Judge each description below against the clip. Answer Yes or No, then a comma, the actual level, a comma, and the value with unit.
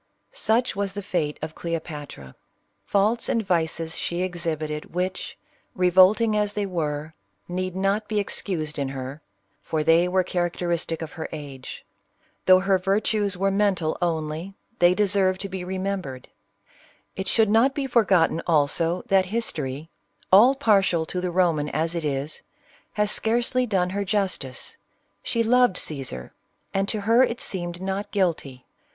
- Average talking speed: Yes, average, 150 wpm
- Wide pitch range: No, average, 4.0 semitones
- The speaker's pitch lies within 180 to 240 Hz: Yes, medium, 185 Hz